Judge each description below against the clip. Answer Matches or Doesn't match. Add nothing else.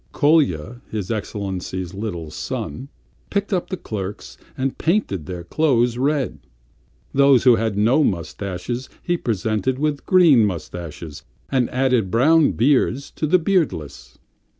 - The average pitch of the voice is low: Matches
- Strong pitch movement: Matches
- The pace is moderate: Doesn't match